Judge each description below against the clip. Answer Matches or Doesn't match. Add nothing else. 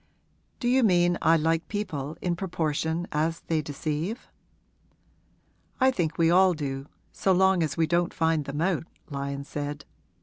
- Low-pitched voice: Doesn't match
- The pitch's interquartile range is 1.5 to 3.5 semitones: Matches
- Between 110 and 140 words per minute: Doesn't match